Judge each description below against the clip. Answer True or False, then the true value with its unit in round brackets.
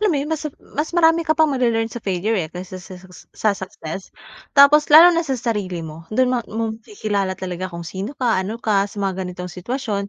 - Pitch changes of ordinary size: False (6.8 semitones)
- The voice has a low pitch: False (215 Hz)